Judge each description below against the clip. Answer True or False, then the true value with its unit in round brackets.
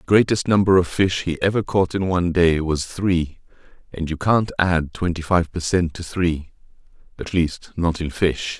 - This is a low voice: True (85 Hz)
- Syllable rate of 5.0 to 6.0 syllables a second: False (4.6 syllables/s)